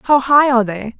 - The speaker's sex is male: No, female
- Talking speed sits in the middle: No, fast, 240 wpm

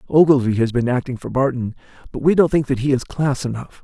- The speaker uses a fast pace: Yes, fast, 235 wpm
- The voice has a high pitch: No, low, 130 Hz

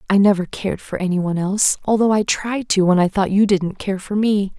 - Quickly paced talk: Yes, fast, 225 wpm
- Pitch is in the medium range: No, high, 195 Hz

